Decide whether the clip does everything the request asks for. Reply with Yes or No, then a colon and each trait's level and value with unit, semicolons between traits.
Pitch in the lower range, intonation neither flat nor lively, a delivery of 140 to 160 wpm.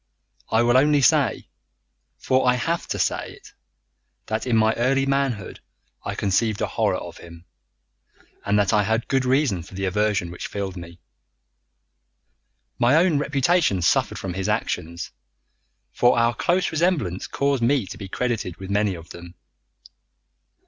No: low, 110 Hz; wide, 5.9 semitones; average, 155 wpm